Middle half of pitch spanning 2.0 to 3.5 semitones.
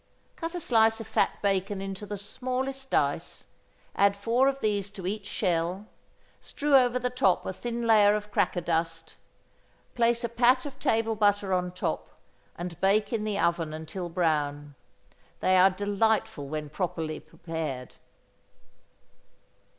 No: average, 4.6 semitones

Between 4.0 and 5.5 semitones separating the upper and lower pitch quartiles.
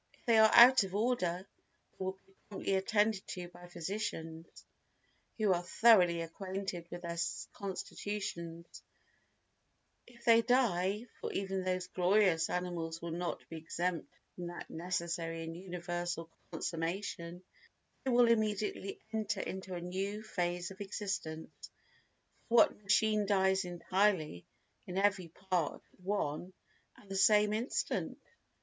No: average, 3.1 semitones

